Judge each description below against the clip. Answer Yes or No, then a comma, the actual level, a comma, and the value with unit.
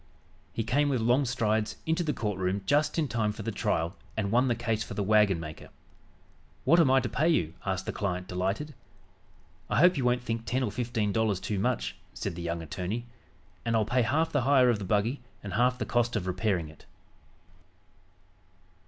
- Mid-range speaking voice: No, low, 115 Hz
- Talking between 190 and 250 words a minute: Yes, average, 200 wpm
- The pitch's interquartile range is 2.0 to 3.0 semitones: No, average, 4.6 semitones